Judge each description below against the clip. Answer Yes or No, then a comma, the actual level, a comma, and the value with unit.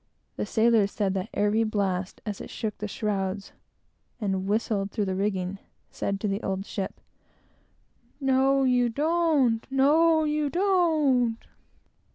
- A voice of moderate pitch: No, high, 220 Hz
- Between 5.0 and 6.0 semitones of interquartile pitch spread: Yes, wide, 5.6 semitones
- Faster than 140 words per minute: No, slow, 135 wpm